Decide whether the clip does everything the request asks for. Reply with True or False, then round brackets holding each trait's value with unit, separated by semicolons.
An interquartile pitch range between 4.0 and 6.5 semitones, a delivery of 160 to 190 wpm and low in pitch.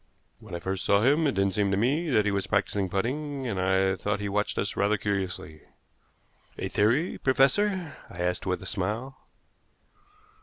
True (5.5 semitones; 180 wpm; 105 Hz)